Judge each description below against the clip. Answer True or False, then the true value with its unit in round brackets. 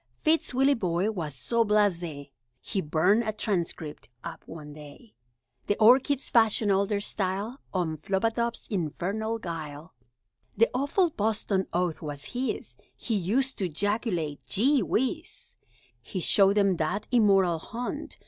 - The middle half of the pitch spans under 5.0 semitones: False (5.3 semitones)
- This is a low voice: False (200 Hz)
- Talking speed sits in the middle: False (130 wpm)